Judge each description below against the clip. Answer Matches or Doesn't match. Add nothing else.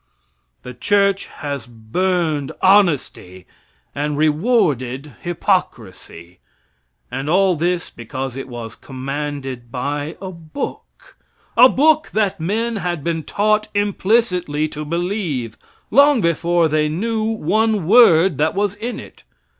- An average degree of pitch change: Doesn't match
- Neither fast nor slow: Doesn't match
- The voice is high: Doesn't match